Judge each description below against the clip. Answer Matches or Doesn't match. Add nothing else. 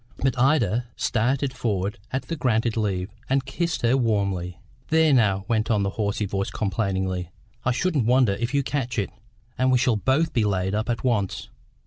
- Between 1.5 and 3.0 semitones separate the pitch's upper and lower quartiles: Doesn't match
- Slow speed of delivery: Doesn't match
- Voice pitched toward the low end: Matches